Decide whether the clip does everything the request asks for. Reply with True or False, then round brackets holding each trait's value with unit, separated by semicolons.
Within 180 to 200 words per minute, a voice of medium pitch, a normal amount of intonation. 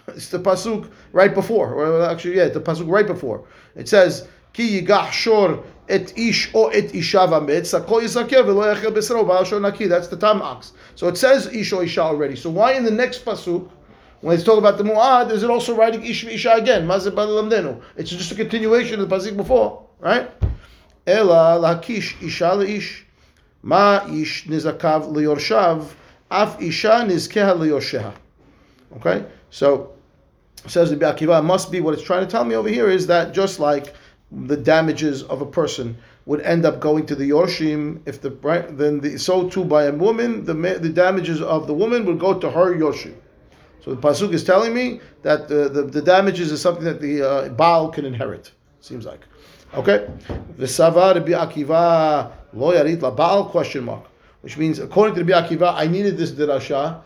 True (185 wpm; 175 Hz; 4.7 semitones)